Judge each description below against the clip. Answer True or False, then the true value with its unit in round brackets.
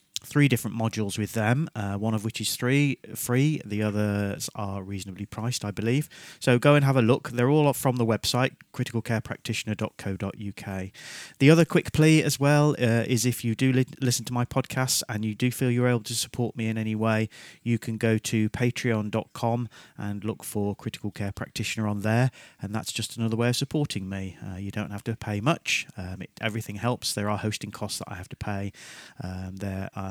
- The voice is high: False (115 Hz)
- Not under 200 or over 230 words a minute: True (205 wpm)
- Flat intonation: False (3.2 semitones)